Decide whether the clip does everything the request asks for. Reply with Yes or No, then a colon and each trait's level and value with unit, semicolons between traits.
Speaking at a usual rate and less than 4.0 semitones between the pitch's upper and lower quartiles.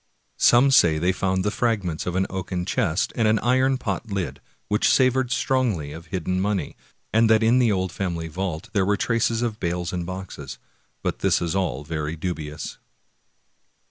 No: average, 175 wpm; average, 4.7 semitones